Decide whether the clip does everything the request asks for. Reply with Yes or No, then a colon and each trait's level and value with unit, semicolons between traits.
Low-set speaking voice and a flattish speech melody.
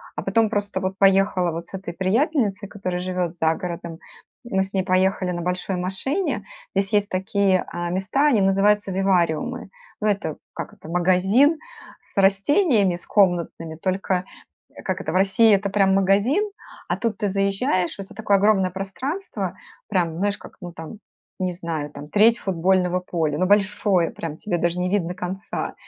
No: high, 190 Hz; narrow, 2.3 semitones